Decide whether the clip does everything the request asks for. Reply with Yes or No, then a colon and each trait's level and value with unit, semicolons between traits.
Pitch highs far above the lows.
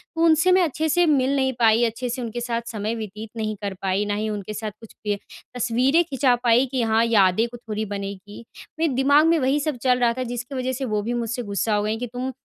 No: average, 3.6 semitones